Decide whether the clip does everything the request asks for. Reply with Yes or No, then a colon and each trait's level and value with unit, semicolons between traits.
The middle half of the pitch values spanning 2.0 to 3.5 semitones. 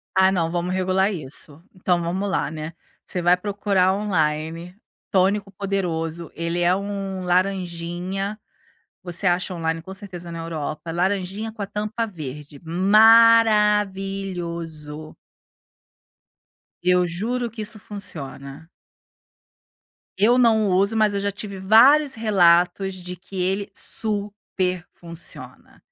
Yes: average, 3.1 semitones